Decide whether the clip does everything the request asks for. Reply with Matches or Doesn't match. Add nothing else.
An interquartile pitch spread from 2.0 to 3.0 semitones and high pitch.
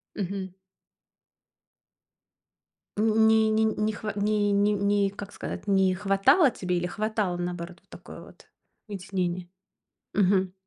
Matches